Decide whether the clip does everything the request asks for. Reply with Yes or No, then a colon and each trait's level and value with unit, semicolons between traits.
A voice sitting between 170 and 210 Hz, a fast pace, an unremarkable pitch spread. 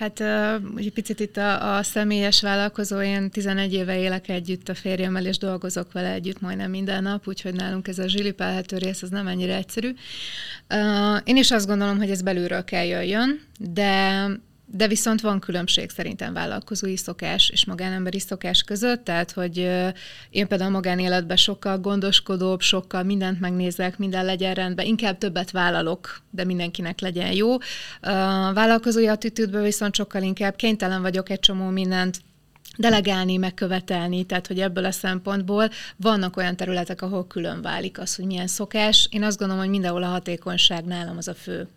No: high, 190 Hz; fast, 165 wpm; narrow, 1.9 semitones